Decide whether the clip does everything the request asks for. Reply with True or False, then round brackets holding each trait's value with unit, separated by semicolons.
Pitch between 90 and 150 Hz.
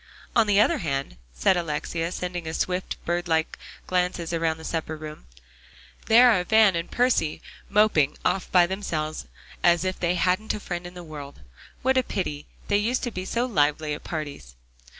False (175 Hz)